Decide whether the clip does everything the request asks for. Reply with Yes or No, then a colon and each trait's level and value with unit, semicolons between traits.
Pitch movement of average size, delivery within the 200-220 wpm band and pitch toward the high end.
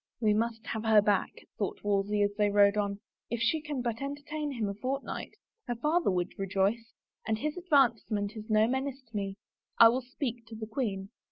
Yes: average, 4.1 semitones; fast, 205 wpm; high, 225 Hz